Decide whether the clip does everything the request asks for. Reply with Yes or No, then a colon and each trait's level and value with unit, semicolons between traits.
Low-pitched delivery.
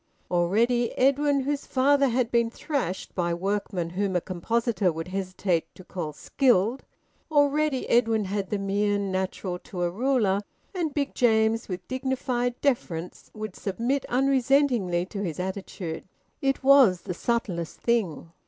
No: high, 215 Hz